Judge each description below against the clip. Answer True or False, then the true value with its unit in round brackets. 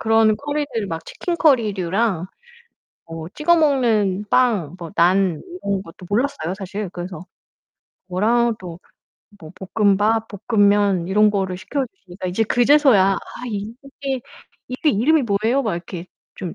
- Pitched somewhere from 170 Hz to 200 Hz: False (210 Hz)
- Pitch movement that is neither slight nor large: True (4.9 semitones)